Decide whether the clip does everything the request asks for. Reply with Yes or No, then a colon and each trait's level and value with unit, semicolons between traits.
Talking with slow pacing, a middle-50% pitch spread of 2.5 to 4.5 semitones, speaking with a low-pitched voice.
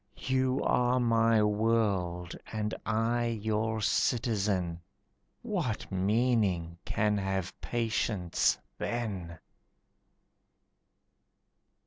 Yes: slow, 70 wpm; average, 3.4 semitones; low, 110 Hz